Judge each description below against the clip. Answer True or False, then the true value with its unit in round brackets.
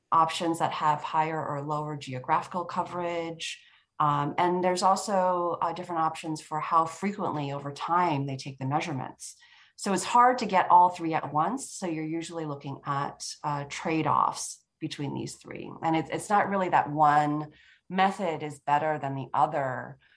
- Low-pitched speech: False (160 Hz)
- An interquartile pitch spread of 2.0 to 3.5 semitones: True (2.9 semitones)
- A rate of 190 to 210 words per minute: False (170 wpm)